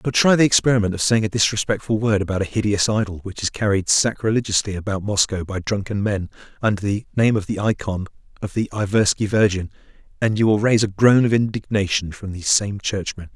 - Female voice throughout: No, male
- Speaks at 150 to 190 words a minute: No, average, 200 wpm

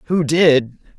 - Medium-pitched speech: Yes, medium, 150 Hz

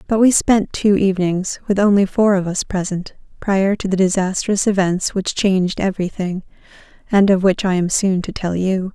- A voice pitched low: No, high, 190 Hz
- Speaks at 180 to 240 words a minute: Yes, average, 190 wpm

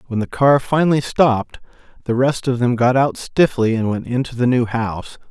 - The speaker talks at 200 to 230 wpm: Yes, fast, 205 wpm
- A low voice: Yes, low, 125 Hz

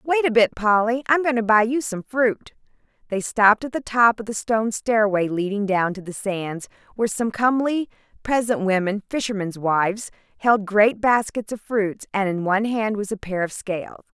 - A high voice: Yes, high, 215 Hz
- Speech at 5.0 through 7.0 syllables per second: Yes, 5.1 syllables/s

